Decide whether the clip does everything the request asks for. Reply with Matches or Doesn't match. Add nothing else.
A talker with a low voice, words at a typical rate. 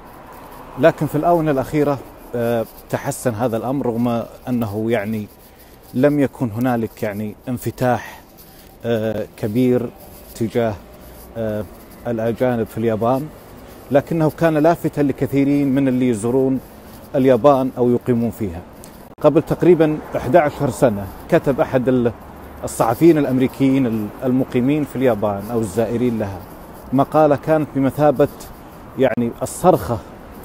Matches